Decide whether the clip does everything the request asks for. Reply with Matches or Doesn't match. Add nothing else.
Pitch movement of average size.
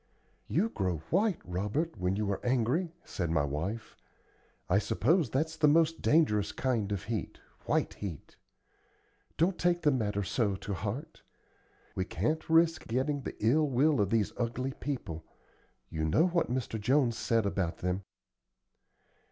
Doesn't match